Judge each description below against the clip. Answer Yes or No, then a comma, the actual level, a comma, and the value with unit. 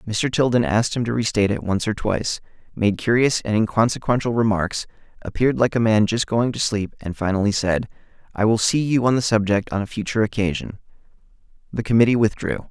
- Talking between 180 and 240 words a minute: Yes, average, 190 wpm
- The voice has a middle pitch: No, low, 110 Hz